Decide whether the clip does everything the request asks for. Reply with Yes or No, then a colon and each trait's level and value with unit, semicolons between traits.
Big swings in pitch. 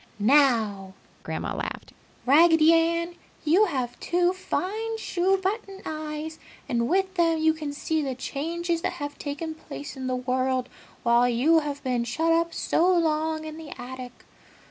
No: average, 4.5 semitones